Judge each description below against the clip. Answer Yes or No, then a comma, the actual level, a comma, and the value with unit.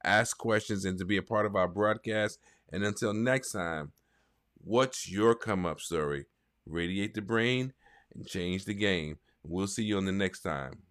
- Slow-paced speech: No, average, 180 wpm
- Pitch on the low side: Yes, low, 100 Hz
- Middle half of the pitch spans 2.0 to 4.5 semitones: Yes, average, 3.0 semitones